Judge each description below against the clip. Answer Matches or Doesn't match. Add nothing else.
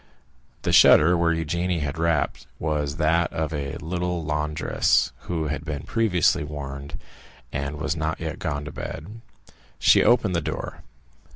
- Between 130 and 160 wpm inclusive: Matches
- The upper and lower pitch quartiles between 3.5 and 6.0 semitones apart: Doesn't match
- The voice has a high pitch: Doesn't match